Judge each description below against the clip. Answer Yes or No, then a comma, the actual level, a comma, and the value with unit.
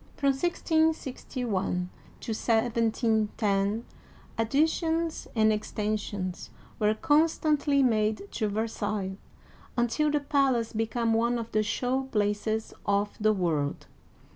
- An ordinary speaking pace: No, slow, 115 wpm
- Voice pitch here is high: Yes, high, 225 Hz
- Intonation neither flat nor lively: Yes, average, 4.2 semitones